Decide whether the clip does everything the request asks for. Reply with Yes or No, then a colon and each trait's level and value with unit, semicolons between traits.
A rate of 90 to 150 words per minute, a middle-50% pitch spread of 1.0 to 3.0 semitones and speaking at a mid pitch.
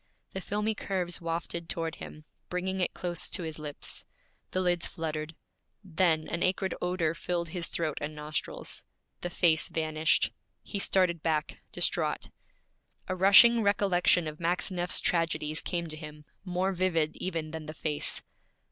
Yes: average, 145 wpm; average, 2.7 semitones; medium, 170 Hz